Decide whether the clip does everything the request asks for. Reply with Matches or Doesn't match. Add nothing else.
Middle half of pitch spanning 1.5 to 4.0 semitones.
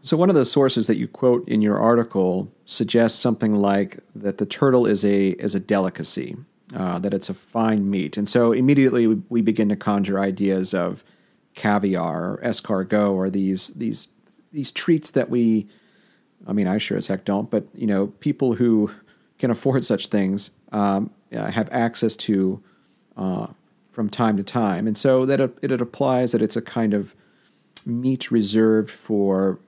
Matches